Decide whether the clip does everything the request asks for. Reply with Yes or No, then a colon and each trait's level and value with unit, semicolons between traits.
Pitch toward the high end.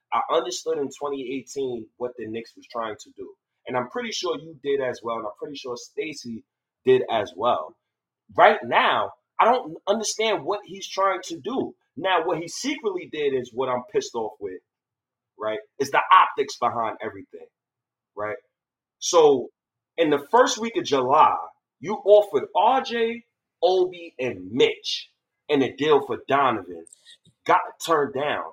Yes: high, 230 Hz